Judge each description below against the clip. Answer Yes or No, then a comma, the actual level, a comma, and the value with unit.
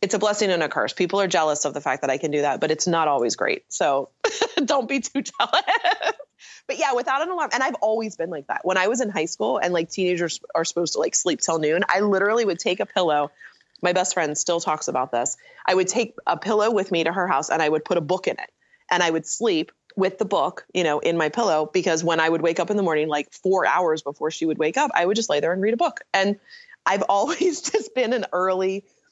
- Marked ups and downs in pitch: Yes, wide, 5.7 semitones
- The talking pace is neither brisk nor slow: No, fast, 270 wpm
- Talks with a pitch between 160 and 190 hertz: Yes, medium, 185 Hz